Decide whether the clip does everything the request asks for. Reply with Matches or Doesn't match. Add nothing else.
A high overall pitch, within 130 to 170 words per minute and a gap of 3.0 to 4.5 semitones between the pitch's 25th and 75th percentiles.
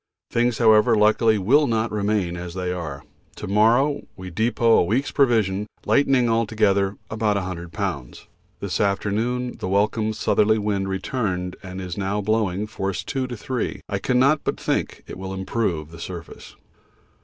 Doesn't match